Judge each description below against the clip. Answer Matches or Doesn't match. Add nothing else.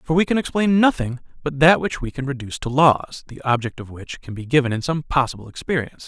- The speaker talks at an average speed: Doesn't match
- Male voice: Matches